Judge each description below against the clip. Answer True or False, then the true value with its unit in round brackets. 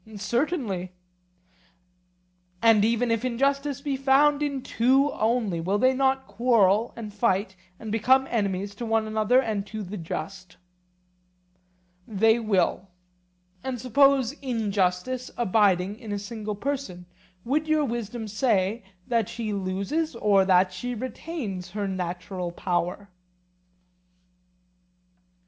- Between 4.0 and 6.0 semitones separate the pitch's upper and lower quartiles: True (4.6 semitones)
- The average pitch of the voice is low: False (220 Hz)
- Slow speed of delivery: True (120 wpm)